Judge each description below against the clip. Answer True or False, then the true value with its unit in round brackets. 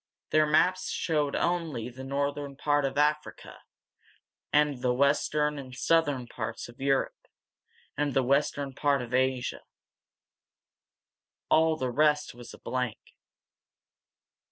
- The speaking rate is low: True (115 wpm)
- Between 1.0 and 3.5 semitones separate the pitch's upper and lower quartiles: True (2.6 semitones)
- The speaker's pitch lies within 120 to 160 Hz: True (140 Hz)